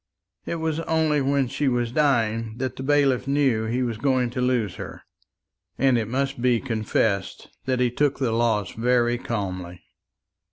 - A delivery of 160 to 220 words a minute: Yes, average, 165 wpm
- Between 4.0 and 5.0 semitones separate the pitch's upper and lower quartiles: No, average, 3.1 semitones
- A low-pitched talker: Yes, low, 125 Hz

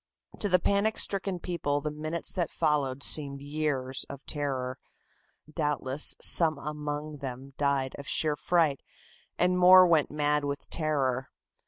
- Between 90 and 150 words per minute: Yes, average, 140 wpm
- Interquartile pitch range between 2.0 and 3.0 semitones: Yes, average, 2.7 semitones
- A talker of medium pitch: Yes, medium, 150 Hz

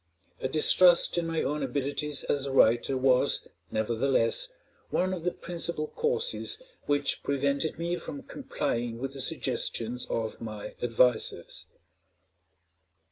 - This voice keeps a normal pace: No, slow, 125 wpm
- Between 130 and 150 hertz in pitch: Yes, medium, 140 Hz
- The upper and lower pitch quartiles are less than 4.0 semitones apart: No, wide, 5.4 semitones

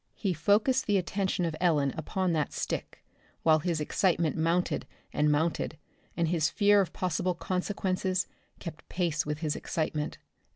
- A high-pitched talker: No, medium, 170 Hz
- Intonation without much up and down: No, average, 3.1 semitones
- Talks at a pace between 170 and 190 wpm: No, average, 150 wpm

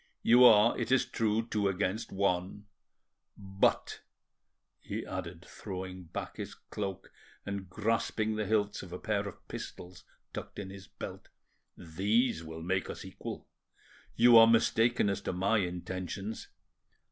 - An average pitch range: Yes, average, 3.0 semitones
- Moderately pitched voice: No, low, 100 Hz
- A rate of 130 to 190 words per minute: Yes, average, 140 wpm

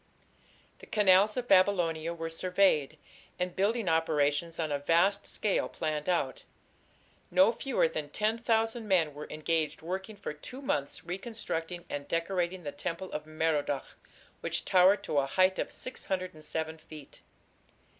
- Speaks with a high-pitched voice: No, medium, 175 Hz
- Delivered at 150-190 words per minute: No, average, 140 wpm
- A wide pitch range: No, average, 4.1 semitones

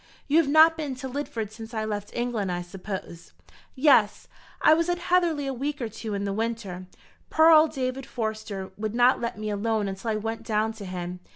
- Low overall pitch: No, high, 225 Hz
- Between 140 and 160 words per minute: No, fast, 205 wpm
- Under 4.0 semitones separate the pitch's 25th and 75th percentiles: No, average, 4.9 semitones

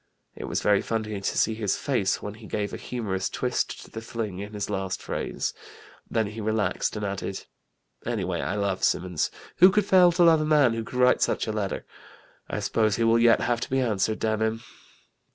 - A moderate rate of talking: No, fast, 210 wpm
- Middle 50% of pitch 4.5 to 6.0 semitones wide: No, average, 2.9 semitones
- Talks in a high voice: No, low, 110 Hz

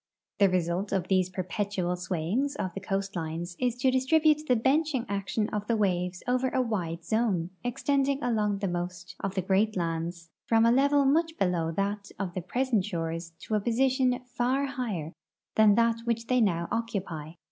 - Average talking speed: Yes, average, 175 wpm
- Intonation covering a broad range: Yes, wide, 5.7 semitones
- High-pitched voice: Yes, high, 205 Hz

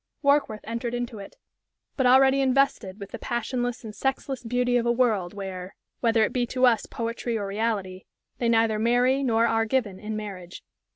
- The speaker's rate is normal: Yes, average, 180 wpm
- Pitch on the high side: Yes, high, 230 Hz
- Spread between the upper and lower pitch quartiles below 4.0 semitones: Yes, average, 2.7 semitones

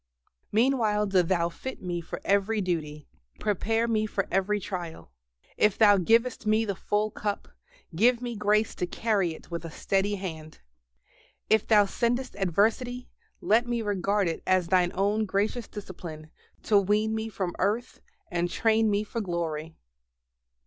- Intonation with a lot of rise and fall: No, average, 3.6 semitones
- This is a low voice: No, high, 205 Hz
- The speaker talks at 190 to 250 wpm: No, average, 155 wpm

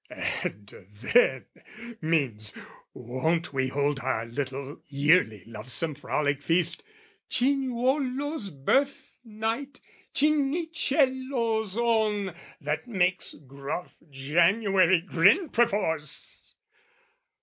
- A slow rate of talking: Yes, slow, 80 wpm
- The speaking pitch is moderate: Yes, medium, 180 Hz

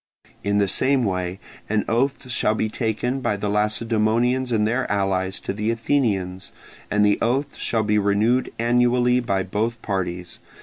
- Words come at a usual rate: Yes, average, 160 wpm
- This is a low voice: Yes, low, 110 Hz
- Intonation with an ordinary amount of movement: Yes, average, 3.3 semitones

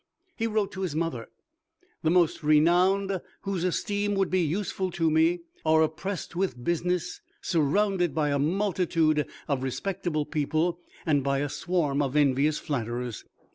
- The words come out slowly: No, average, 145 wpm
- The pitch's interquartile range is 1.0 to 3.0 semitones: No, average, 4.0 semitones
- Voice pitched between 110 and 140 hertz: No, medium, 165 Hz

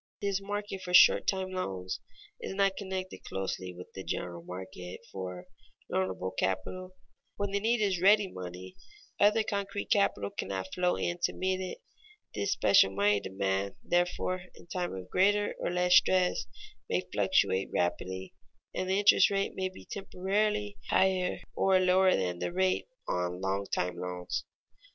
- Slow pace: No, average, 155 wpm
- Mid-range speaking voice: Yes, medium, 180 Hz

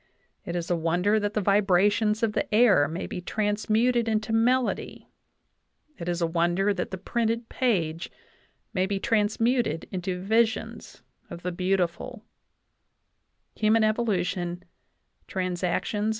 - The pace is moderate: No, slow, 125 wpm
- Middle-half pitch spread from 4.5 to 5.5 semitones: No, average, 4.0 semitones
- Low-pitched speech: No, high, 205 Hz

